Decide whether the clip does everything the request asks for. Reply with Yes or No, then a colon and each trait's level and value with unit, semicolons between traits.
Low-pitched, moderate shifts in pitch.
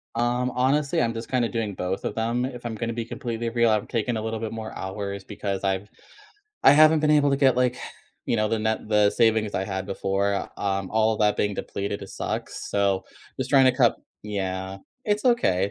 Yes: low, 110 Hz; average, 3.6 semitones